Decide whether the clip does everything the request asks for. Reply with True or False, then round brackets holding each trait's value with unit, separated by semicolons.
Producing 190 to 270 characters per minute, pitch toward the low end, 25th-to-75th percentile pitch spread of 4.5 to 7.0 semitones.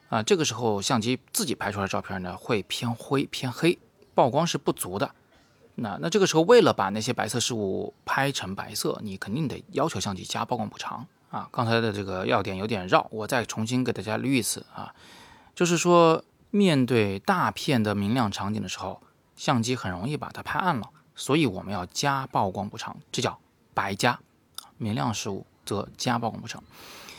False (285 characters per minute; 115 Hz; 5.2 semitones)